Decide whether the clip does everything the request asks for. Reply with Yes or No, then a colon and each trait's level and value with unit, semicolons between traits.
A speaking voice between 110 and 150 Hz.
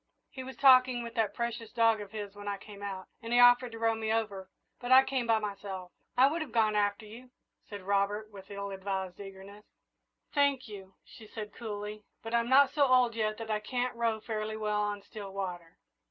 No: high, 215 Hz